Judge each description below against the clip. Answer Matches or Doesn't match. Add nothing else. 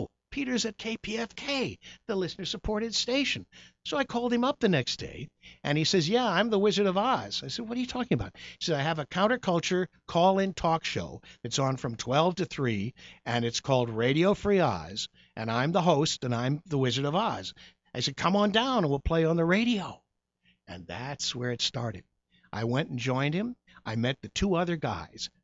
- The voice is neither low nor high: Matches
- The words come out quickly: Matches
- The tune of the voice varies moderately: Doesn't match